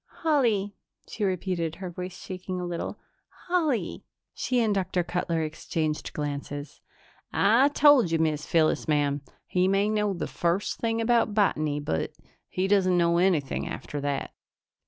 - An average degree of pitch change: Yes, average, 4.7 semitones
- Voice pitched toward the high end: No, medium, 180 Hz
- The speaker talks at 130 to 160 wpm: Yes, average, 145 wpm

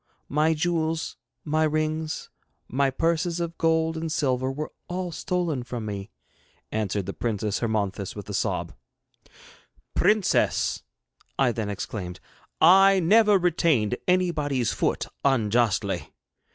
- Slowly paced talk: Yes, slow, 115 wpm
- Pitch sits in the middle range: Yes, medium, 155 Hz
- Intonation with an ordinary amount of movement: No, wide, 6.3 semitones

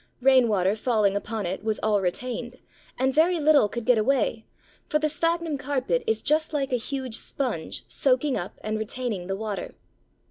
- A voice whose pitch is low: No, very high, 250 Hz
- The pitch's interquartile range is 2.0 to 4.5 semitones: No, average, 4.9 semitones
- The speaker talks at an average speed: Yes, average, 170 wpm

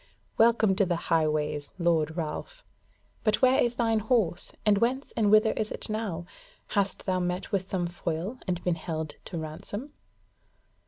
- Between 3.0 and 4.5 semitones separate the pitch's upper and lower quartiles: No, average, 5.0 semitones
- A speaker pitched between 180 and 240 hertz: Yes, high, 190 Hz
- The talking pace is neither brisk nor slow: Yes, average, 160 wpm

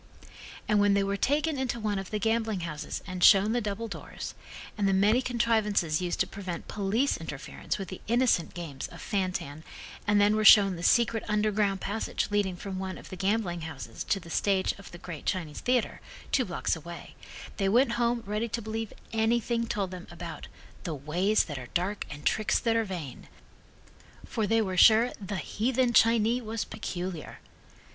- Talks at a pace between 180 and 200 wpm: Yes, average, 185 wpm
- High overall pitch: Yes, high, 205 Hz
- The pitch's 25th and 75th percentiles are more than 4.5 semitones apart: No, average, 3.6 semitones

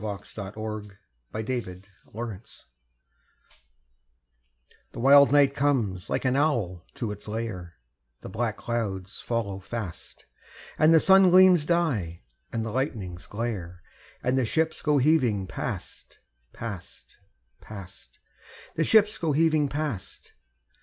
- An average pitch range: No, wide, 6.6 semitones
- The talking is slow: Yes, slow, 125 wpm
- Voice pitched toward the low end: Yes, low, 115 Hz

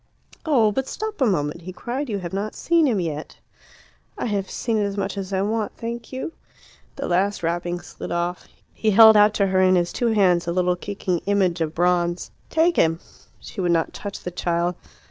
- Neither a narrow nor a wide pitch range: Yes, average, 3.9 semitones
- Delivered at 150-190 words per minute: No, fast, 205 wpm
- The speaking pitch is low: No, high, 195 Hz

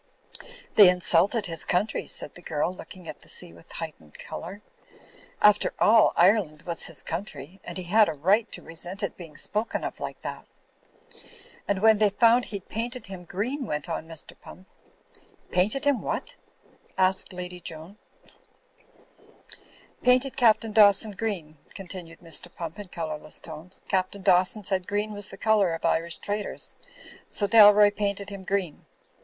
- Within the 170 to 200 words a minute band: No, average, 160 wpm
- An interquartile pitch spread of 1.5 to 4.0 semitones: Yes, average, 3.7 semitones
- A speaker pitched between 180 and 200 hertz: Yes, high, 190 Hz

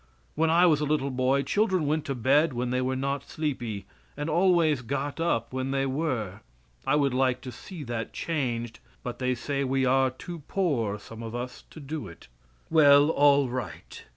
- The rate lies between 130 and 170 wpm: No, average, 190 wpm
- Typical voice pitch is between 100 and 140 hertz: Yes, low, 135 Hz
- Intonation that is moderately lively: Yes, average, 3.5 semitones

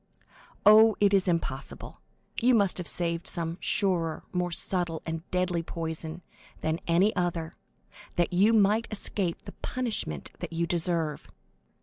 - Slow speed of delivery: Yes, slow, 130 wpm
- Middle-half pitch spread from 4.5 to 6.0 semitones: No, average, 3.2 semitones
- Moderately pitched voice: Yes, medium, 175 Hz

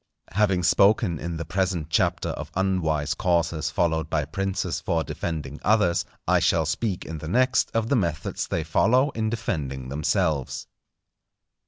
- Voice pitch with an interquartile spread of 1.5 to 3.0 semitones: No, average, 3.8 semitones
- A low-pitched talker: Yes, very low, 85 Hz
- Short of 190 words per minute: Yes, average, 150 wpm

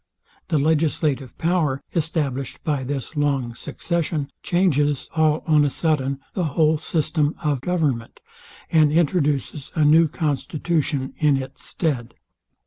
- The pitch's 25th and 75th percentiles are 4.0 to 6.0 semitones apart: No, average, 2.7 semitones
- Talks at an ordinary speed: No, slow, 125 wpm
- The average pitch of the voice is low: No, medium, 150 Hz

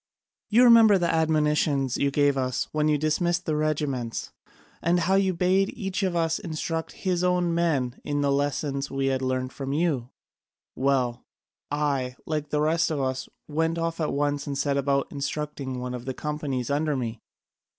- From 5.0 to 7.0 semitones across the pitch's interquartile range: No, average, 3.3 semitones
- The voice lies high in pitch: No, medium, 150 Hz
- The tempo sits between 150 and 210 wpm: Yes, average, 175 wpm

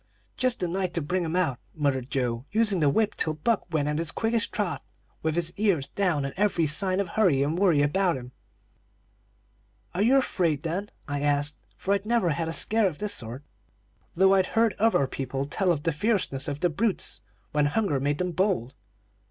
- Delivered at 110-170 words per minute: No, average, 200 wpm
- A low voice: No, medium, 170 Hz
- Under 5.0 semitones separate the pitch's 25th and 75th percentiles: No, wide, 5.5 semitones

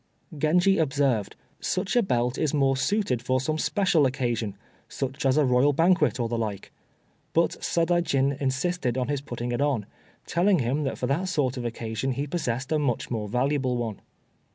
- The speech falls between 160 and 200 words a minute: Yes, average, 175 wpm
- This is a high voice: No, low, 135 Hz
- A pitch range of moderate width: Yes, average, 3.9 semitones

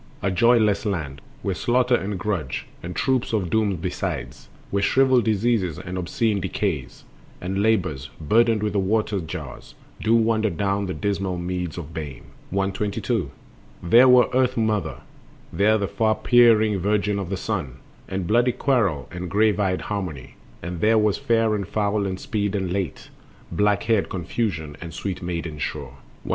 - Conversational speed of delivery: Yes, average, 160 wpm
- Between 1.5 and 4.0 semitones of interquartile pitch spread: Yes, average, 3.5 semitones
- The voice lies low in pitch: Yes, low, 100 Hz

